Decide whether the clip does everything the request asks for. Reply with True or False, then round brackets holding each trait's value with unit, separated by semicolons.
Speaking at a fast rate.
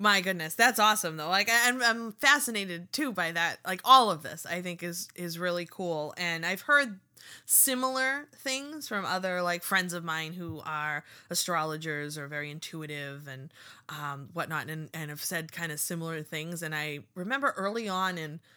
False (180 wpm)